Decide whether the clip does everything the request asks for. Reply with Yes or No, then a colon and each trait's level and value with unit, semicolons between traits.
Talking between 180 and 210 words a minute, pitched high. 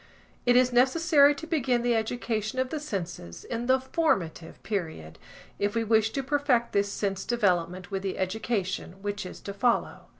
No: average, 170 wpm; high, 220 Hz